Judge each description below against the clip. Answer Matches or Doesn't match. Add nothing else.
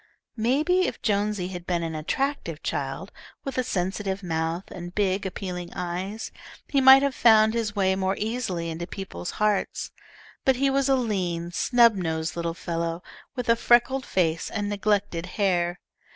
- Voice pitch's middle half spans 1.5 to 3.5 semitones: Doesn't match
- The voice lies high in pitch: Matches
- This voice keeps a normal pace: Matches